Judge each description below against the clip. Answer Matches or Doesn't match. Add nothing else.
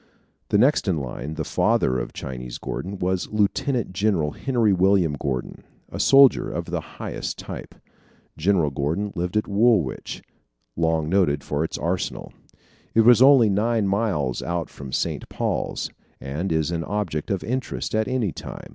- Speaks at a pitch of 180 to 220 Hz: Doesn't match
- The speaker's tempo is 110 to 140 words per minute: Doesn't match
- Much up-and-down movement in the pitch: Matches